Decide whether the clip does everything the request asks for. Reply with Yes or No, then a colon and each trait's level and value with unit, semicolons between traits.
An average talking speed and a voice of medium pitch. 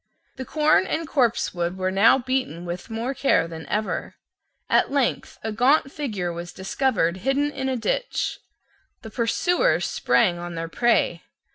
No: average, 150 wpm; high, 230 Hz